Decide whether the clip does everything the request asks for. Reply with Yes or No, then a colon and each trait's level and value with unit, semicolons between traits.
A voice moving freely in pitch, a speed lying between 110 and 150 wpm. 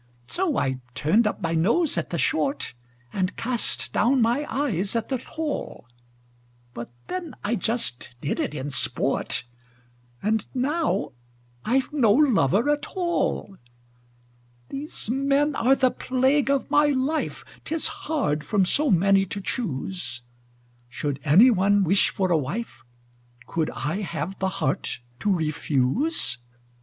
Yes: wide, 8.9 semitones; slow, 135 wpm